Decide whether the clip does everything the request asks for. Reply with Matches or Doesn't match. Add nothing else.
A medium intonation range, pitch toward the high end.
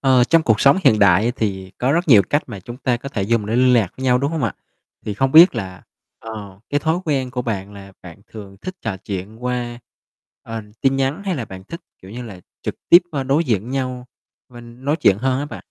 Doesn't match